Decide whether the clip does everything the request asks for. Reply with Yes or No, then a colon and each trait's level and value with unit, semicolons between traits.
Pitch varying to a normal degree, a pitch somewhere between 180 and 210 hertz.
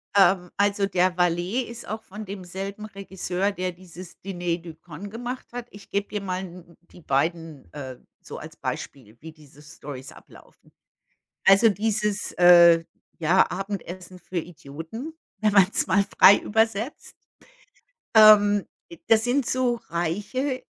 Yes: average, 3.4 semitones; high, 190 Hz